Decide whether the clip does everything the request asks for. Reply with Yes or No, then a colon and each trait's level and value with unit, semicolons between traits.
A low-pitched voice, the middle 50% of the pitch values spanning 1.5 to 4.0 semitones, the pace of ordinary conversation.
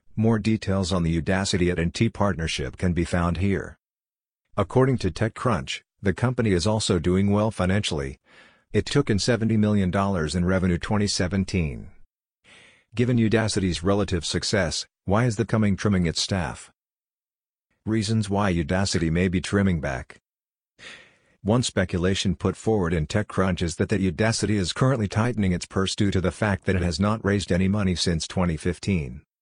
Yes: very low, 95 Hz; average, 3.2 semitones; average, 155 wpm